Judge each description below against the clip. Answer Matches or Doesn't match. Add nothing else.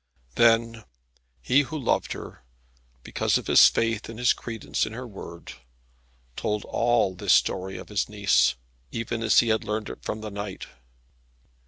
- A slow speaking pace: Doesn't match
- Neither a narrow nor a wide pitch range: Doesn't match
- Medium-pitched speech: Doesn't match